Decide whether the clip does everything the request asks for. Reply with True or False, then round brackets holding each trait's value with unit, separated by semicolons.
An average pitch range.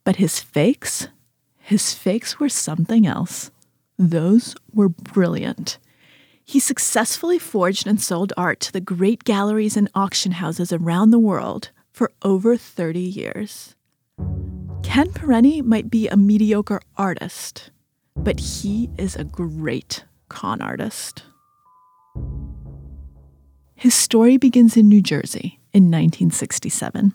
True (4.8 semitones)